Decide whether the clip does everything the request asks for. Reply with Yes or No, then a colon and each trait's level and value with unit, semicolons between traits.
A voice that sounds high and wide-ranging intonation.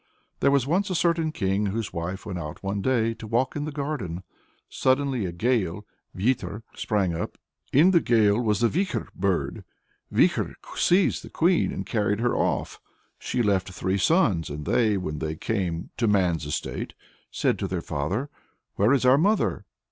No: low, 110 Hz; wide, 6.3 semitones